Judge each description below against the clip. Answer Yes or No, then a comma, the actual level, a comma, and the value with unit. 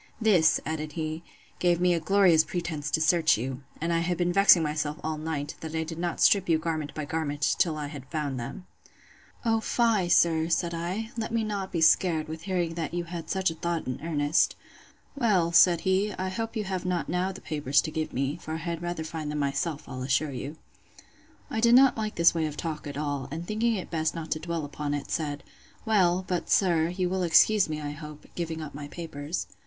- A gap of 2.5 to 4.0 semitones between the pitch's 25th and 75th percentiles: Yes, average, 2.9 semitones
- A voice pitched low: No, medium, 165 Hz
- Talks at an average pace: No, fast, 220 wpm